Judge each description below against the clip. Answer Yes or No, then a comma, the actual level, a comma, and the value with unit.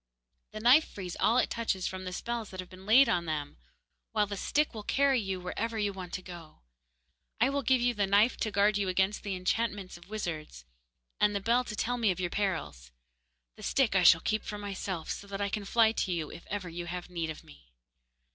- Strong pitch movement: No, average, 3.5 semitones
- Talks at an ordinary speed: No, fast, 230 wpm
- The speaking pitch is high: Yes, high, 200 Hz